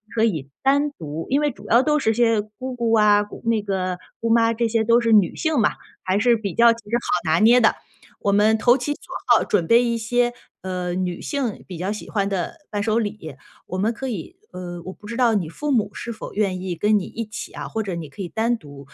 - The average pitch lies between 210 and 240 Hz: Yes, high, 215 Hz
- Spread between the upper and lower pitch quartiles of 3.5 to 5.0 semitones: Yes, average, 3.9 semitones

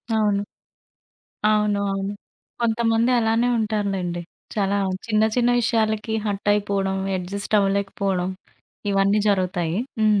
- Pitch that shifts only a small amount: Yes, narrow, 1.9 semitones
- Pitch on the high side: Yes, high, 205 Hz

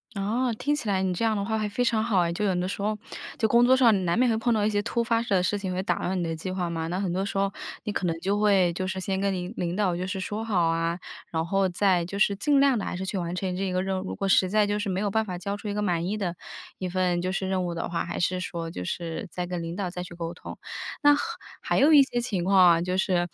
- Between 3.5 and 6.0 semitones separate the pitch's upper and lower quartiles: No, average, 2.8 semitones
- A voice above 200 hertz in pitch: No, high, 190 Hz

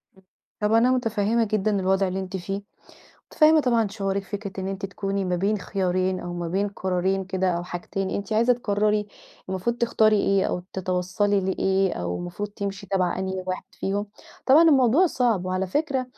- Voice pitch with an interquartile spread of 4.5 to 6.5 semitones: No, narrow, 2.4 semitones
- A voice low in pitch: No, high, 195 Hz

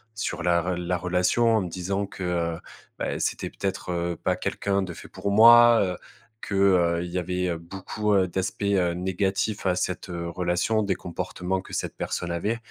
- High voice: No, very low, 90 Hz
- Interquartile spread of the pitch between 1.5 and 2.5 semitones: Yes, narrow, 2.2 semitones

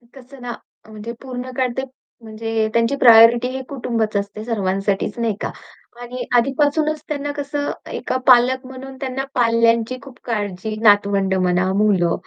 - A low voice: No, high, 235 Hz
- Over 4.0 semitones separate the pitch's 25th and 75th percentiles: No, average, 3.5 semitones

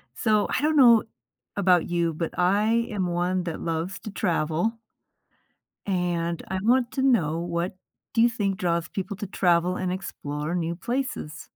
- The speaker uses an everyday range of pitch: Yes, average, 4.1 semitones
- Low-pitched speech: No, medium, 185 Hz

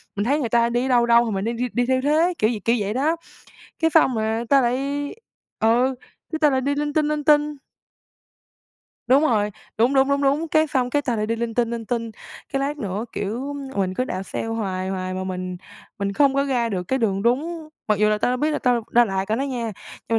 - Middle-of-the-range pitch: No, high, 240 Hz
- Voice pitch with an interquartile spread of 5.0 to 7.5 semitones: No, average, 4.4 semitones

